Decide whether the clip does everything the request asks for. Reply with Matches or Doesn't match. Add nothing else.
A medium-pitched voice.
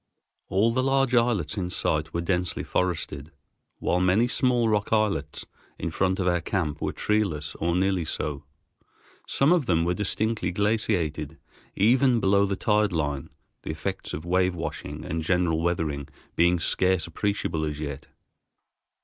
Doesn't match